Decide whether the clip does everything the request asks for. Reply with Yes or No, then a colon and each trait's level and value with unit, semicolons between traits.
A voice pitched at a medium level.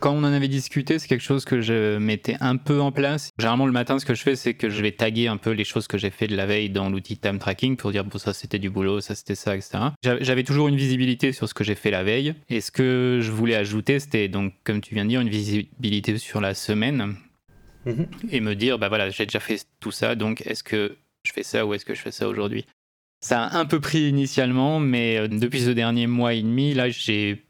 No: low, 115 Hz